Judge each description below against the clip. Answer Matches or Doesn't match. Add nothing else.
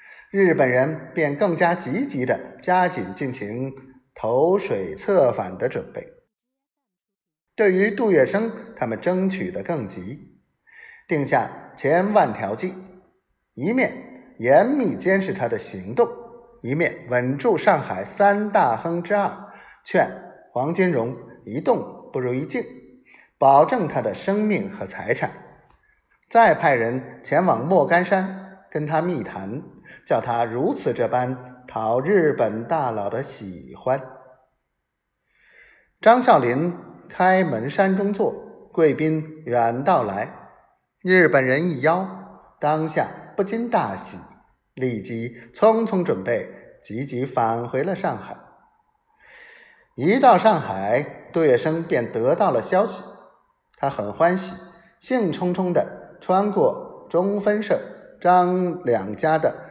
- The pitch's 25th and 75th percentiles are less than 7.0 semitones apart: Doesn't match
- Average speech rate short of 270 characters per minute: Matches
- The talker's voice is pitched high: Doesn't match